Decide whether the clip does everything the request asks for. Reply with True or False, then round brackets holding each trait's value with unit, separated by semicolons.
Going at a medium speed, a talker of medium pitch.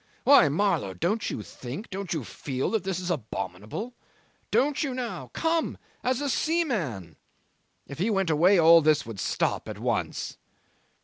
True (160 wpm; 180 Hz)